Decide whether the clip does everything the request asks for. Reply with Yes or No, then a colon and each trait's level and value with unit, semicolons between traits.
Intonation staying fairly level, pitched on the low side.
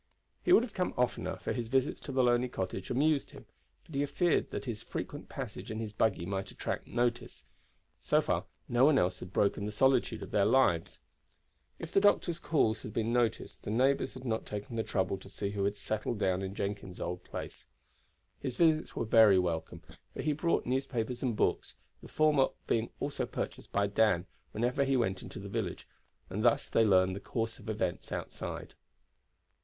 No: average, 4.9 semitones; low, 115 Hz